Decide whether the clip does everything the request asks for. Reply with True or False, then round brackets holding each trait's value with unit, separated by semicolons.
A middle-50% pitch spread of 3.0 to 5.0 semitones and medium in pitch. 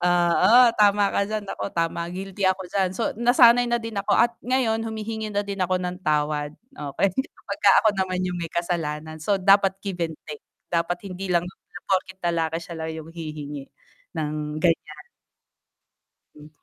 True (3.8 semitones; 180 Hz)